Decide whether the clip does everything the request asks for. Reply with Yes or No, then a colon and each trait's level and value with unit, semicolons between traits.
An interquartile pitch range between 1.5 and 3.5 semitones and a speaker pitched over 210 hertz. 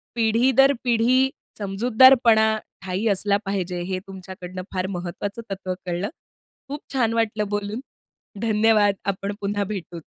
No: average, 3.2 semitones; high, 205 Hz